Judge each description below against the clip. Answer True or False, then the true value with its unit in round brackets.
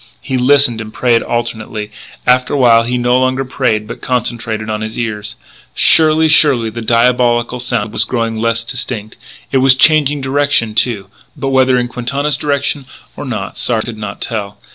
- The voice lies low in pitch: True (120 Hz)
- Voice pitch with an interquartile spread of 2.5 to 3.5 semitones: True (2.9 semitones)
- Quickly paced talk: False (170 wpm)